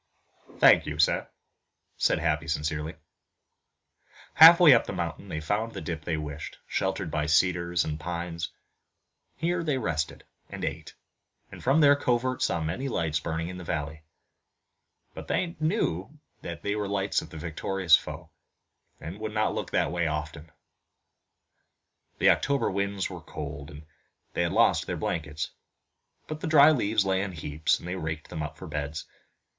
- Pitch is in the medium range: No, very low, 85 Hz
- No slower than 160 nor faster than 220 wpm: Yes, average, 165 wpm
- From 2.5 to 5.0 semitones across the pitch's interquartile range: No, wide, 5.5 semitones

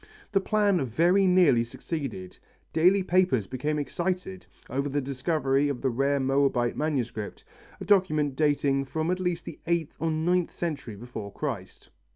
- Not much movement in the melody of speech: No, average, 4.9 semitones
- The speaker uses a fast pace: No, average, 150 wpm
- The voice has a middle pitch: Yes, medium, 145 Hz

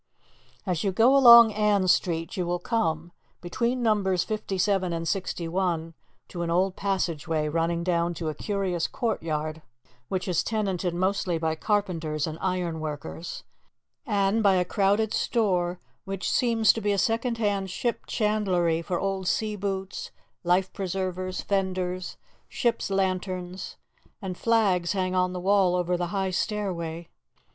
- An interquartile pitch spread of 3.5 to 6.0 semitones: No, average, 2.8 semitones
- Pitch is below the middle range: No, medium, 185 Hz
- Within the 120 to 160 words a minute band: Yes, average, 145 wpm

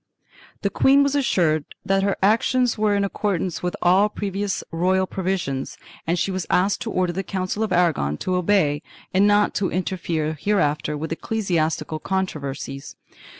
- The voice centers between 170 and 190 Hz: Yes, medium, 185 Hz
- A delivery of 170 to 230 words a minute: No, average, 160 wpm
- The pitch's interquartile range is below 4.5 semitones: Yes, average, 3.8 semitones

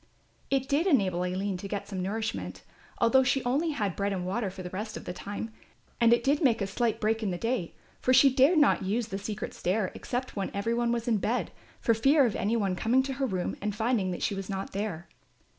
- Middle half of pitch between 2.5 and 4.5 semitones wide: Yes, average, 4.2 semitones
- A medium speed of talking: No, fast, 240 wpm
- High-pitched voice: Yes, high, 220 Hz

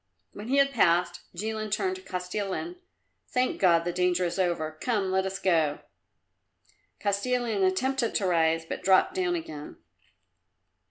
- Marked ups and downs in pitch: Yes, wide, 5.7 semitones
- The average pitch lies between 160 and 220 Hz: Yes, high, 190 Hz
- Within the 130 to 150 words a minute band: Yes, average, 145 wpm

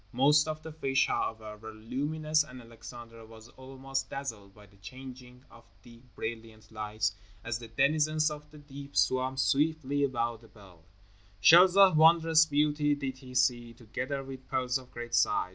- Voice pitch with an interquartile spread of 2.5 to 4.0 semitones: No, average, 4.4 semitones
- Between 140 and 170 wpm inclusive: Yes, average, 165 wpm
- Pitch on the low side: Yes, low, 130 Hz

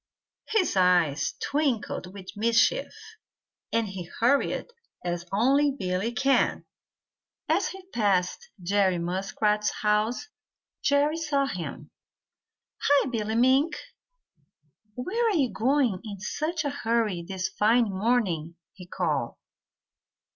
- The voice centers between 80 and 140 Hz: No, high, 220 Hz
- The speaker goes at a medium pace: No, slow, 110 wpm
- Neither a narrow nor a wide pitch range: No, wide, 6.8 semitones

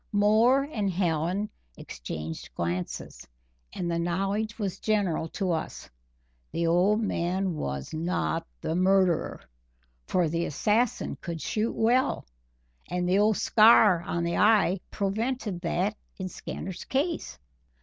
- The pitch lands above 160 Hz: Yes, high, 190 Hz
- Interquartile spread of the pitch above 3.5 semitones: Yes, average, 4.0 semitones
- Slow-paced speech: Yes, slow, 125 wpm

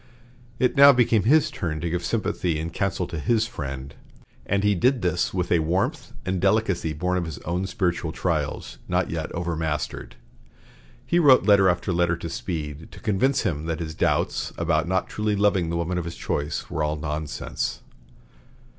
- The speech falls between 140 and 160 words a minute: No, average, 180 wpm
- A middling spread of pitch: Yes, average, 4.0 semitones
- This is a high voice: No, very low, 90 Hz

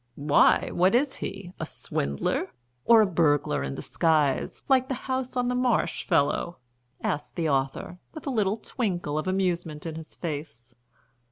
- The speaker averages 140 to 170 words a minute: Yes, average, 160 wpm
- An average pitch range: No, wide, 7.6 semitones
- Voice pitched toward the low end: No, medium, 175 Hz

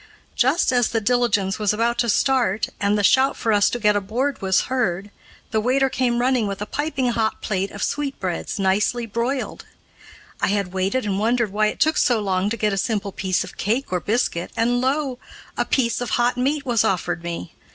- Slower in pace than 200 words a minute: No, fast, 205 wpm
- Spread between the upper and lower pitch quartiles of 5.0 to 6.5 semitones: No, average, 3.9 semitones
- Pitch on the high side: Yes, high, 225 Hz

